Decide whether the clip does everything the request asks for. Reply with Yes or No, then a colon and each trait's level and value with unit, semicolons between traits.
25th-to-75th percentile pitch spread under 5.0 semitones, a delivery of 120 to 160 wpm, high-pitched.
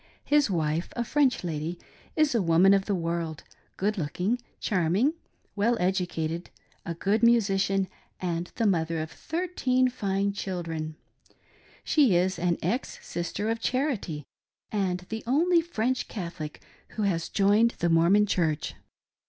No: average, 5.3 semitones; average, 145 wpm; high, 195 Hz